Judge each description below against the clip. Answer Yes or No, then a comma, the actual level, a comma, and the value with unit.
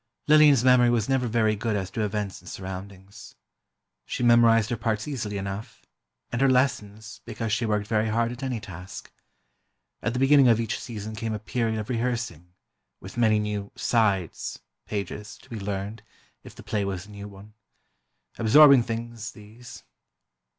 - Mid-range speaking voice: No, low, 110 Hz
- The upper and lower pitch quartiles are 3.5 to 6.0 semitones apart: No, narrow, 2.6 semitones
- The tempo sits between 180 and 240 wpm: No, average, 165 wpm